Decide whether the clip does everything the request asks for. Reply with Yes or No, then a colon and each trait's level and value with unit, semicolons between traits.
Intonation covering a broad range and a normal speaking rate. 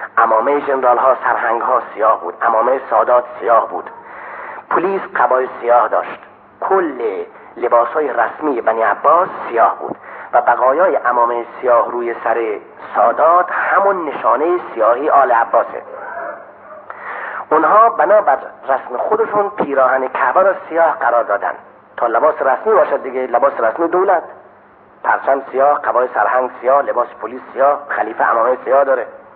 Yes: wide, 6.1 semitones; average, 130 wpm